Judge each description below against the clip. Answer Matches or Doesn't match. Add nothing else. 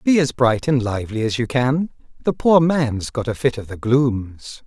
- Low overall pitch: Matches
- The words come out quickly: Matches